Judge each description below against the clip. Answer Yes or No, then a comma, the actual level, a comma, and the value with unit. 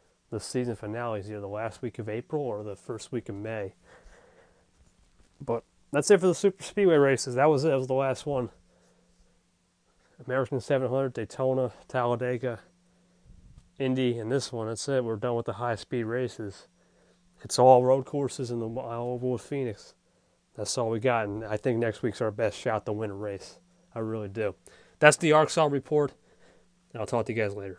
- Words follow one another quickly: No, average, 190 wpm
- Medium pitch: No, low, 125 Hz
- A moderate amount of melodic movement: Yes, average, 3.5 semitones